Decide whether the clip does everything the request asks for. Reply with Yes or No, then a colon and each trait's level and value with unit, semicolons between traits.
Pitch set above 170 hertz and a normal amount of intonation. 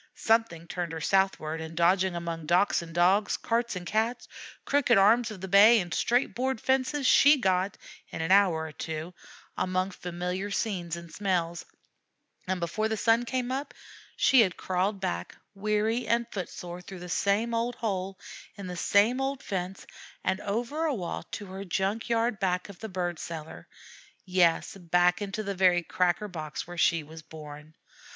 Yes: high, 190 Hz; average, 4.1 semitones